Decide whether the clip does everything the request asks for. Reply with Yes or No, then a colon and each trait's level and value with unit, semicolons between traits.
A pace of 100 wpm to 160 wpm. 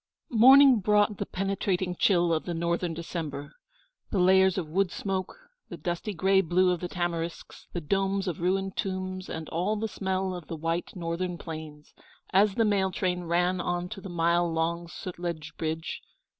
No: average, 170 wpm